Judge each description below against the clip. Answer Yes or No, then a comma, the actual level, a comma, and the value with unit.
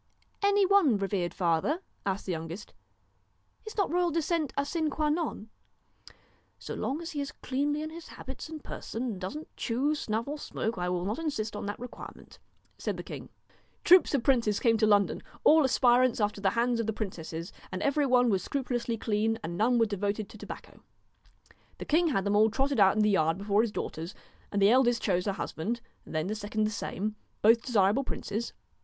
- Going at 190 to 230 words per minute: Yes, fast, 205 wpm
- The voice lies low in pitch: No, high, 230 Hz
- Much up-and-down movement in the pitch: Yes, wide, 5.8 semitones